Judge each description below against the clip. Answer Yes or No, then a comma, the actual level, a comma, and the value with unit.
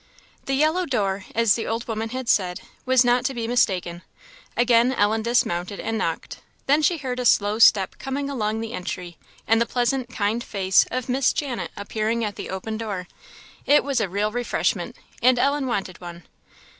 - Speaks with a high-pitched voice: Yes, high, 230 Hz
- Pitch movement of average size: Yes, average, 3.8 semitones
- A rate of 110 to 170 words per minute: No, average, 180 wpm